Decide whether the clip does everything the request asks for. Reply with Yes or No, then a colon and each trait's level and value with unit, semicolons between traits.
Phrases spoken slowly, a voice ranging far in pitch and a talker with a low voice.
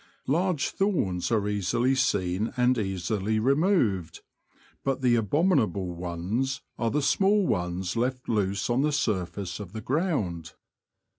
Yes: slow, 130 wpm; wide, 6.4 semitones; low, 115 Hz